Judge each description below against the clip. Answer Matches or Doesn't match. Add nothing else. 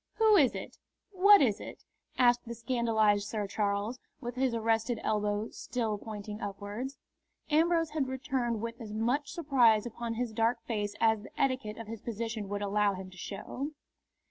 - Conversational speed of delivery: Matches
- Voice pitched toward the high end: Matches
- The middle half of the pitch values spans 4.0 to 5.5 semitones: Doesn't match